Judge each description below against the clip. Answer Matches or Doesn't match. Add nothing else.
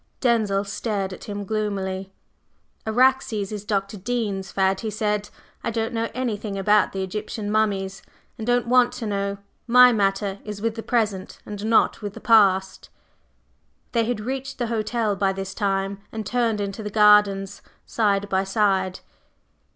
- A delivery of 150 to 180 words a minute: Matches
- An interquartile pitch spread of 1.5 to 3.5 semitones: Matches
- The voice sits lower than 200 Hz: Doesn't match